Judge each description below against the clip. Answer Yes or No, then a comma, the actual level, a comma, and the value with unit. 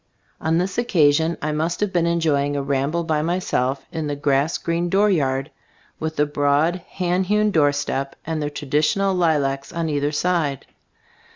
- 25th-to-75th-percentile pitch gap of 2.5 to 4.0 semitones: Yes, average, 3.2 semitones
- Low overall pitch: No, medium, 155 Hz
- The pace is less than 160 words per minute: No, average, 165 wpm